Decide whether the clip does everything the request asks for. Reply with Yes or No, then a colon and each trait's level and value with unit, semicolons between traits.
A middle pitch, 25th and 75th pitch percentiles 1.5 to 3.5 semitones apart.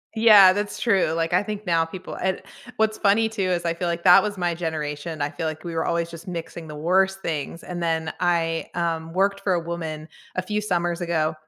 Yes: medium, 170 Hz; average, 2.8 semitones